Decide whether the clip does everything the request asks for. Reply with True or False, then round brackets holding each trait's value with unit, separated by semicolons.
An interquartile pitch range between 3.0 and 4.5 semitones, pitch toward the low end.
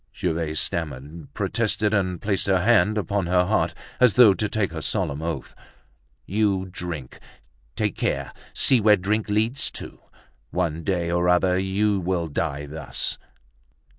True (4.0 semitones; 95 Hz)